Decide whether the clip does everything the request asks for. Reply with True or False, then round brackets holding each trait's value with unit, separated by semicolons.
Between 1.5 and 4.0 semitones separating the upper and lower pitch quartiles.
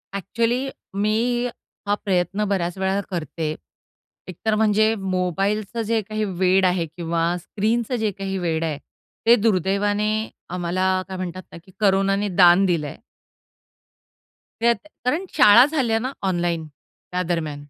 True (3.5 semitones)